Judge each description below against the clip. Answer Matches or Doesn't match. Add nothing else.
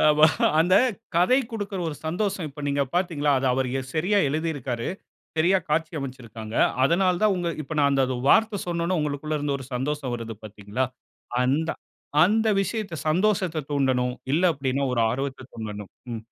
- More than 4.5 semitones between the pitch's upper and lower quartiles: Matches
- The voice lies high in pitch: Doesn't match